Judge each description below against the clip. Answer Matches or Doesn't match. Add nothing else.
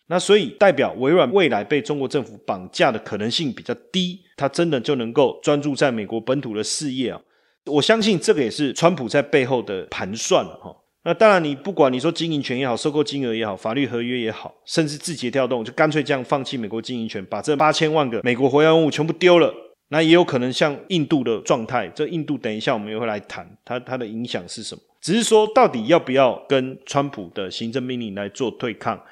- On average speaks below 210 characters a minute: Doesn't match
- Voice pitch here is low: Doesn't match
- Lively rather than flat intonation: Doesn't match